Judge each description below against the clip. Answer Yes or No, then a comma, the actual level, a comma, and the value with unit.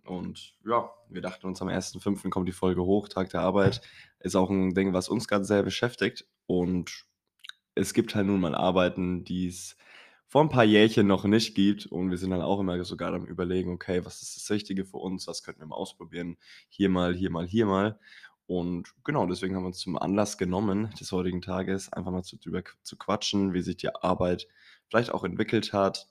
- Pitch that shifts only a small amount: Yes, narrow, 2.0 semitones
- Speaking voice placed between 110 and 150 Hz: No, very low, 95 Hz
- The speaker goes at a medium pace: No, fast, 210 wpm